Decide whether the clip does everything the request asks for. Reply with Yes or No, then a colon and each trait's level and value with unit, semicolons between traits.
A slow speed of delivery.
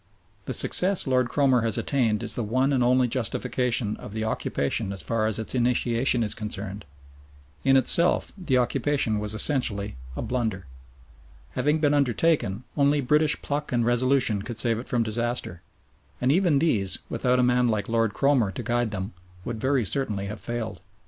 No: average, 170 wpm